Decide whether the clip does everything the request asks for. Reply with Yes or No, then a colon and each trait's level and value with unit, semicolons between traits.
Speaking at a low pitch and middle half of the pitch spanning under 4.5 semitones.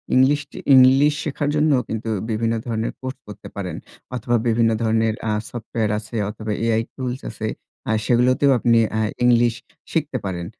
Yes: low, 120 Hz; average, 2.8 semitones